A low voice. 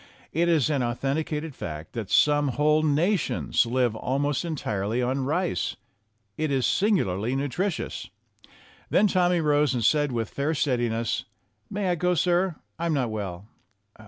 No: medium, 145 Hz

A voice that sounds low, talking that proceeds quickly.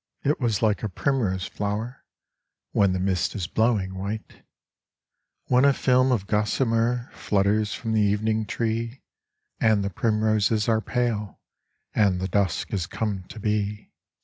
No: low, 105 Hz; average, 145 wpm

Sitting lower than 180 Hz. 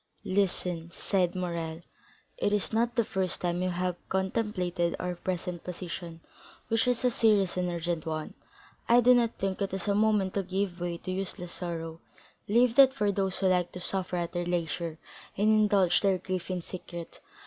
No: medium, 185 Hz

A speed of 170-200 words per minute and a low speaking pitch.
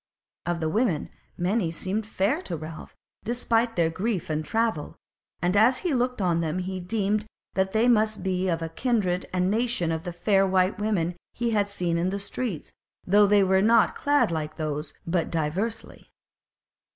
No: average, 175 wpm; high, 190 Hz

